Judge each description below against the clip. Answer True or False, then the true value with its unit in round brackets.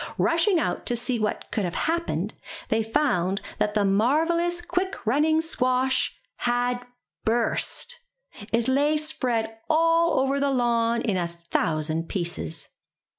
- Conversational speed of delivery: False (130 wpm)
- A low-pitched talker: False (245 Hz)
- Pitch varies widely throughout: True (6.4 semitones)